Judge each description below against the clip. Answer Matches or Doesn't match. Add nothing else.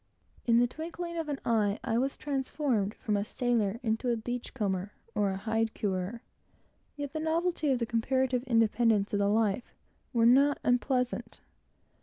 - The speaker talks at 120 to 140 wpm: Doesn't match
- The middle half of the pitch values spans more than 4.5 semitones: Doesn't match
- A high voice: Matches